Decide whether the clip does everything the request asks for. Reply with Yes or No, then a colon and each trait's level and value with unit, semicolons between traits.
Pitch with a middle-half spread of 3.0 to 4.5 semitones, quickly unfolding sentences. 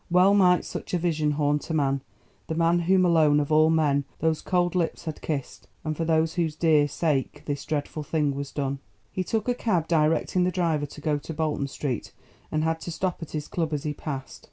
No: narrow, 2.6 semitones; fast, 210 wpm